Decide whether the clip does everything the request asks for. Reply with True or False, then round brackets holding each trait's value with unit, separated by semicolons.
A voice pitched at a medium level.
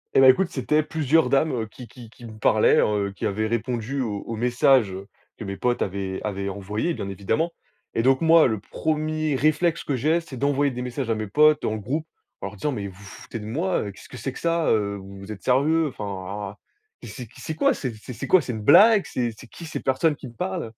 False (125 Hz)